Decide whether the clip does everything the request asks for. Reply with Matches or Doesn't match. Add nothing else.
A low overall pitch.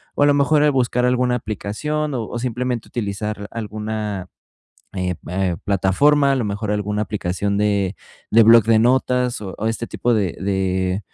Matches